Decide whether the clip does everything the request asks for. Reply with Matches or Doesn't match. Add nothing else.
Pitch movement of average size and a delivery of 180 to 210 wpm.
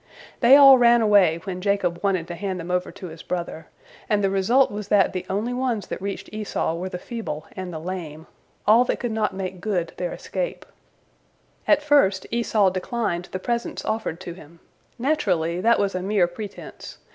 Matches